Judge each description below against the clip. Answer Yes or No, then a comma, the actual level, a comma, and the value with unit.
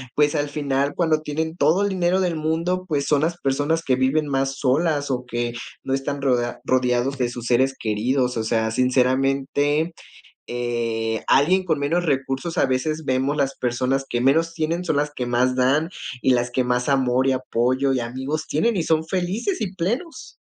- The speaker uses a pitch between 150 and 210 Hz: No, low, 135 Hz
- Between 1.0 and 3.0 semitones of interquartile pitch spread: No, average, 3.8 semitones